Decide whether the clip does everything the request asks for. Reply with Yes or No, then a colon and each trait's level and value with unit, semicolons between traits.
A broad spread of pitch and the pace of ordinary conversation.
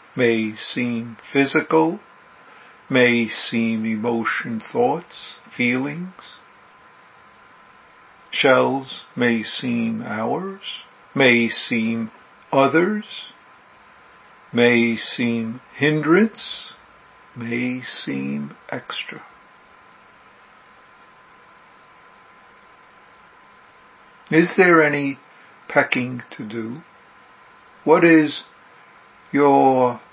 No: wide, 5.7 semitones; slow, 60 wpm